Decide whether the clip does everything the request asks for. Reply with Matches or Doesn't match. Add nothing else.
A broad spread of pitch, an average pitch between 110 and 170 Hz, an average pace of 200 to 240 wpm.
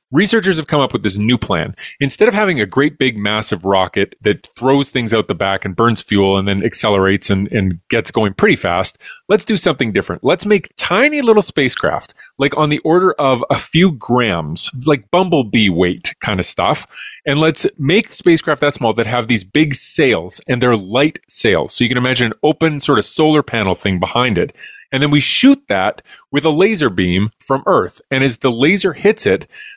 Matches